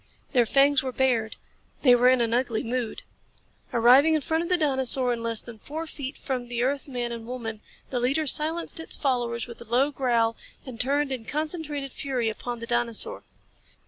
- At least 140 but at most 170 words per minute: No, average, 190 wpm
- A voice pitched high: Yes, very high, 255 Hz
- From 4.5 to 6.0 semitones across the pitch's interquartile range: No, average, 3.2 semitones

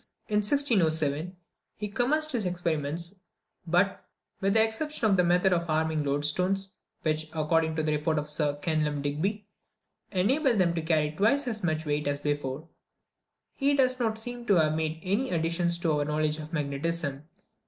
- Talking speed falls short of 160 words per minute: No, average, 165 wpm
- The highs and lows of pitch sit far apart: No, average, 5.0 semitones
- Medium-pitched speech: Yes, medium, 170 Hz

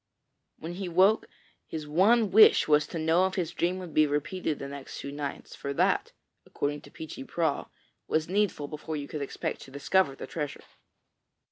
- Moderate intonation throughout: Yes, average, 4.1 semitones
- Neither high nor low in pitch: Yes, medium, 160 Hz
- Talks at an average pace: Yes, average, 180 wpm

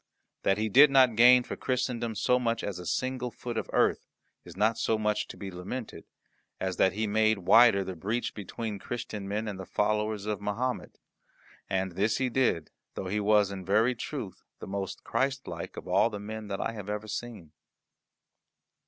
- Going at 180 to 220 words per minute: Yes, average, 190 wpm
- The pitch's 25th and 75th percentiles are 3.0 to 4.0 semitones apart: Yes, average, 3.3 semitones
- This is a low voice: Yes, low, 110 Hz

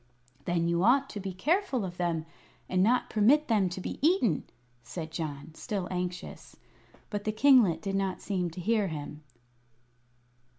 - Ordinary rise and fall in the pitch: Yes, average, 4.6 semitones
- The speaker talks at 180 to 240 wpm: No, average, 160 wpm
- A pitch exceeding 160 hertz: Yes, high, 190 Hz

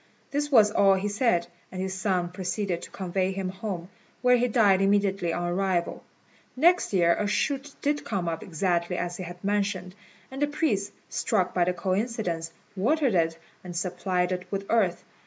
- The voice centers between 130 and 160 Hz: No, high, 190 Hz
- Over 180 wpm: No, average, 175 wpm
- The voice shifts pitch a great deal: No, average, 3.0 semitones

